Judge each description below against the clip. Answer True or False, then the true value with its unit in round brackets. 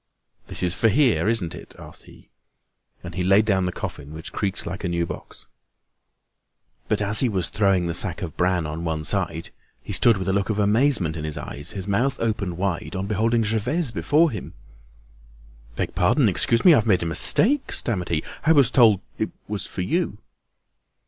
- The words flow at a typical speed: True (195 wpm)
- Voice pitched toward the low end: True (100 Hz)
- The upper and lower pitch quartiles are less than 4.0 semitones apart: False (4.4 semitones)